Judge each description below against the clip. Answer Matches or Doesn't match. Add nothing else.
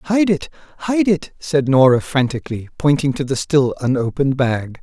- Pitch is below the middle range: Doesn't match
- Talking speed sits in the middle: Matches